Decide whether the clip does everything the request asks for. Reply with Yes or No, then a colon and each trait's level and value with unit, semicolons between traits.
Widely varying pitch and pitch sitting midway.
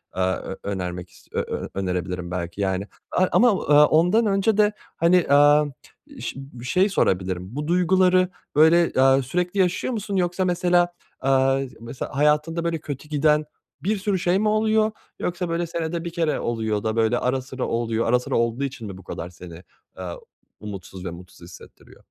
Yes: wide, 8.4 semitones; medium, 145 Hz